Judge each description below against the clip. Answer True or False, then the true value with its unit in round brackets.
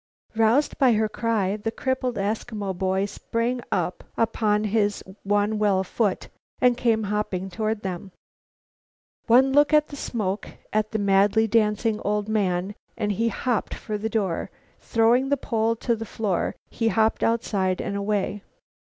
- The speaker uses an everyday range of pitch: False (2.2 semitones)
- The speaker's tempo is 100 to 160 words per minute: True (150 wpm)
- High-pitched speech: True (215 Hz)